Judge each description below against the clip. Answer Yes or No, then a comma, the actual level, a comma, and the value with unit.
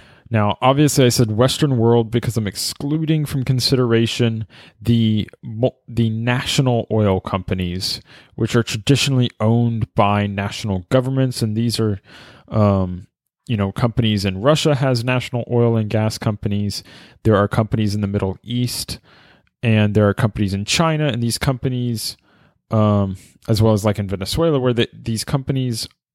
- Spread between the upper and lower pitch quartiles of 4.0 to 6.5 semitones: No, average, 3.2 semitones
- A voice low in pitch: Yes, low, 115 Hz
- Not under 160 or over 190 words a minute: No, average, 150 wpm